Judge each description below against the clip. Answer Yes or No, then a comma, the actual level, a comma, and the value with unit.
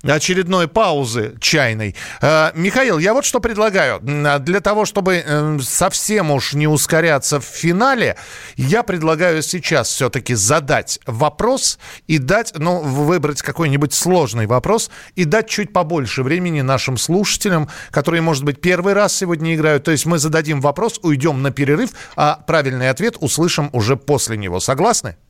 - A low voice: No, medium, 155 Hz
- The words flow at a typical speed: Yes, average, 145 wpm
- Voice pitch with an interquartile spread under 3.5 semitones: No, average, 4.4 semitones